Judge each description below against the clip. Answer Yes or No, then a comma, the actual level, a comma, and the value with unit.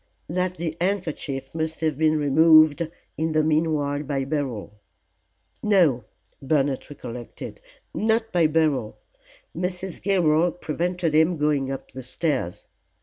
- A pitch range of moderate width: Yes, average, 3.3 semitones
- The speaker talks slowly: Yes, slow, 120 wpm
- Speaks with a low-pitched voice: No, medium, 155 Hz